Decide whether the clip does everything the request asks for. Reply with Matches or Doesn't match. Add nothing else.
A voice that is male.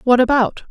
Doesn't match